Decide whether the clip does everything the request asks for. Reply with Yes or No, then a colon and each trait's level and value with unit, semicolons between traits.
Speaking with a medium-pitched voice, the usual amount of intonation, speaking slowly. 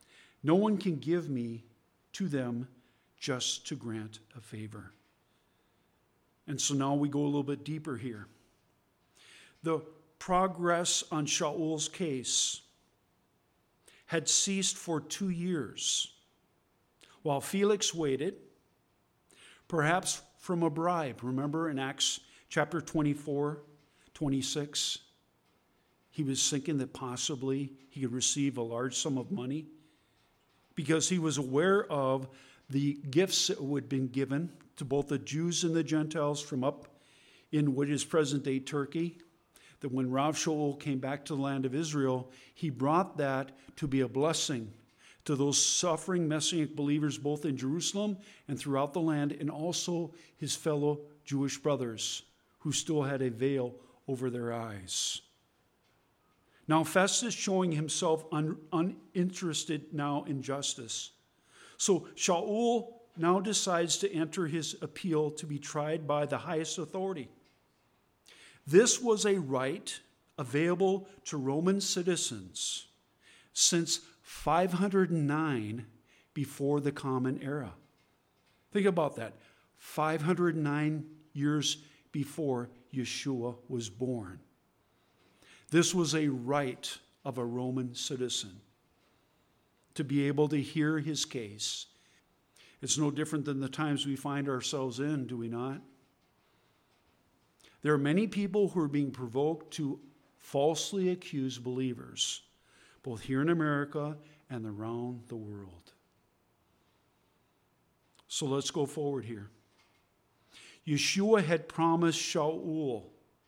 Yes: medium, 145 Hz; average, 3.5 semitones; slow, 125 wpm